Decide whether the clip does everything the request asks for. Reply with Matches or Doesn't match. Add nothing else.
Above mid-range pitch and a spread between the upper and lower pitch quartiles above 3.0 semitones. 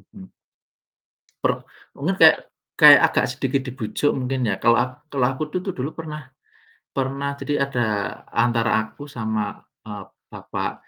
Doesn't match